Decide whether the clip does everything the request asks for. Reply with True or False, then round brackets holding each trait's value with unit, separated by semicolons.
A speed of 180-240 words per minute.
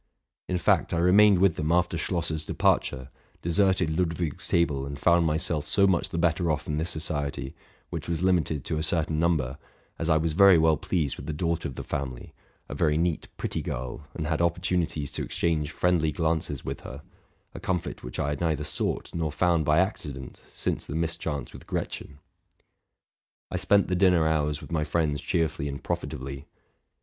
True (190 wpm)